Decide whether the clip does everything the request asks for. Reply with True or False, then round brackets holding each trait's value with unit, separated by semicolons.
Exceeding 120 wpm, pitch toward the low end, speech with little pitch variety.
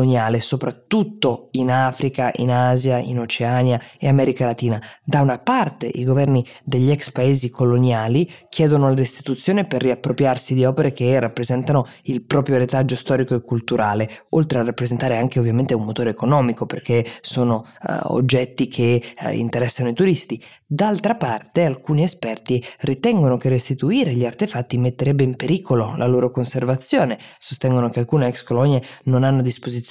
True (150 wpm; 130 Hz; 2.2 semitones)